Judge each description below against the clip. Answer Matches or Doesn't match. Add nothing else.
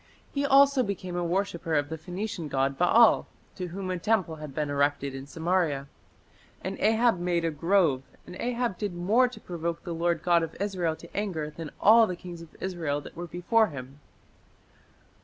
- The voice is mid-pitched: Matches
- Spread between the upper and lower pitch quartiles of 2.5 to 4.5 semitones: Matches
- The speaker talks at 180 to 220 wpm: Matches